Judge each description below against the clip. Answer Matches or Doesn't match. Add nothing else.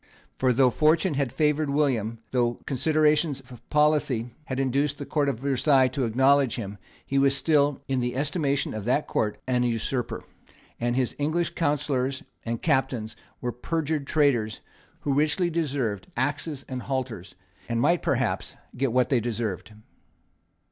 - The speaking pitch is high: Doesn't match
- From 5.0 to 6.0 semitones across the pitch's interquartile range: Doesn't match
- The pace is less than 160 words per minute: Matches